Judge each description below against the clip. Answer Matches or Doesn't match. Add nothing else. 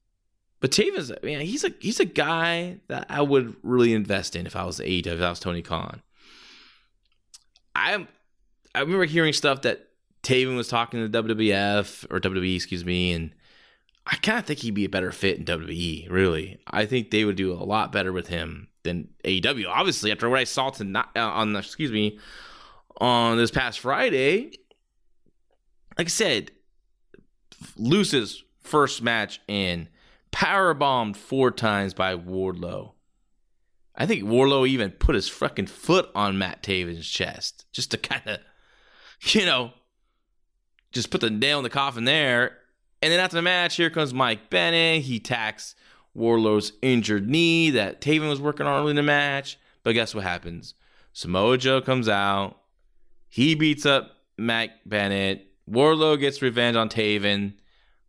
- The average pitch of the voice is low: Matches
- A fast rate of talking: Doesn't match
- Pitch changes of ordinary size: Doesn't match